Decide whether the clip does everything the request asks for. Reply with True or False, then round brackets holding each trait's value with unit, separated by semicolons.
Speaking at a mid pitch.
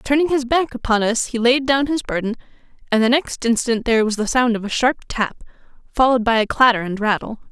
False (240 Hz)